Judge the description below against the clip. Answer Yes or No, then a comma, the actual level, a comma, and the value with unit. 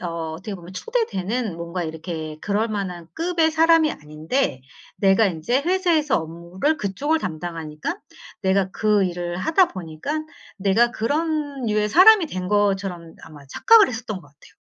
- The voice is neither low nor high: No, high, 200 Hz